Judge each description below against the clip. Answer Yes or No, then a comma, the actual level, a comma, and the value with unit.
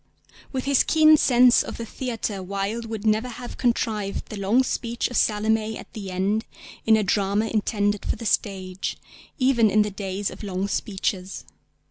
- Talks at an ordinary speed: Yes, average, 170 wpm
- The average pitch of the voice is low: No, high, 215 Hz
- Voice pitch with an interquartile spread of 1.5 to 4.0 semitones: Yes, average, 2.9 semitones